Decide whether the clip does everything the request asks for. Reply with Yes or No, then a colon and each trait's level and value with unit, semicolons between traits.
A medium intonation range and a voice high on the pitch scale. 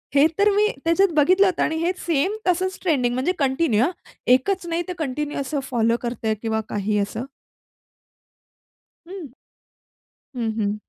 No: wide, 7.1 semitones; very high, 290 Hz